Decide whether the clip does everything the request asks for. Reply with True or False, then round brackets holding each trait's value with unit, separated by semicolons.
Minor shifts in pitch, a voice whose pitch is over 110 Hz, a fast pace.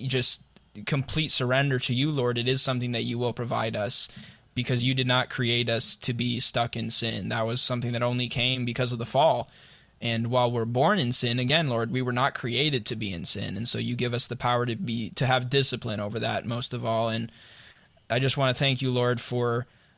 True (1.7 semitones; 120 Hz; 230 wpm)